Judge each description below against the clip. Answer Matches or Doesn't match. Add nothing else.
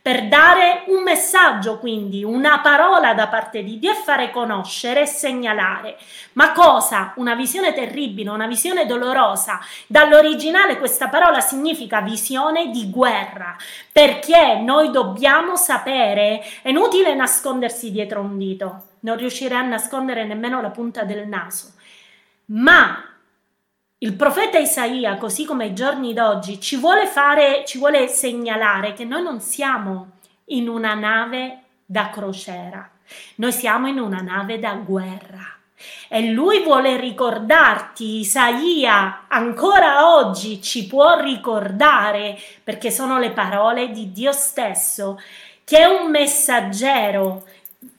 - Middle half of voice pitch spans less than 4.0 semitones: Doesn't match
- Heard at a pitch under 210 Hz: Doesn't match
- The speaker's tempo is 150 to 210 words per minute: Doesn't match